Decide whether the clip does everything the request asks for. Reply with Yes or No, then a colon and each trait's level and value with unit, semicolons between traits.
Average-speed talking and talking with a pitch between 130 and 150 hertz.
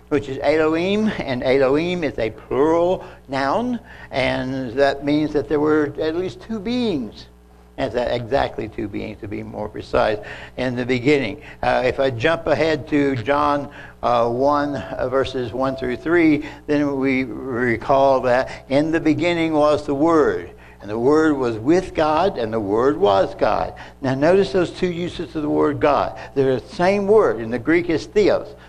Yes: average, 175 wpm; medium, 140 Hz